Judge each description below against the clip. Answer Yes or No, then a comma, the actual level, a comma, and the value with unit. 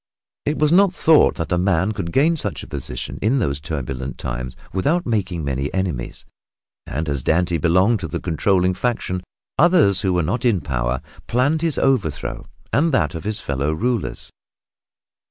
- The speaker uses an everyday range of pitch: No, wide, 8.3 semitones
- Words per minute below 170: No, average, 175 wpm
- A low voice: Yes, very low, 95 Hz